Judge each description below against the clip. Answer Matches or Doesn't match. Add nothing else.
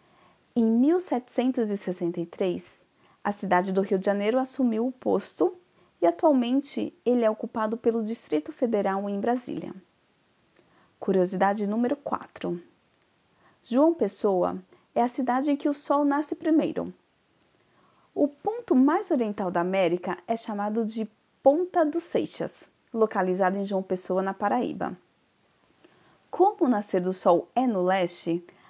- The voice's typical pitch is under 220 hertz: Doesn't match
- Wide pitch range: Matches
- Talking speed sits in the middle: Matches